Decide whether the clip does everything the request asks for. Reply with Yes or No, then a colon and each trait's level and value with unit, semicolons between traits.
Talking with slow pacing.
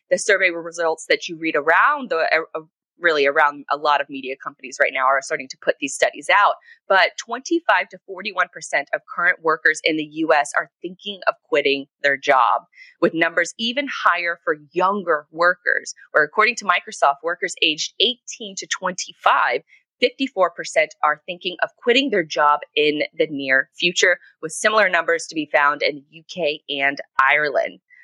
No: average, 175 wpm